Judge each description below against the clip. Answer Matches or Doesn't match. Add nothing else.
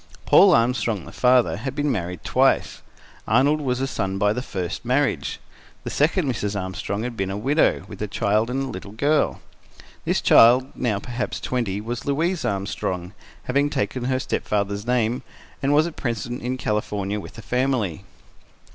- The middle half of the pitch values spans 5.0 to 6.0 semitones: Doesn't match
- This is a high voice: Doesn't match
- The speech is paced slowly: Doesn't match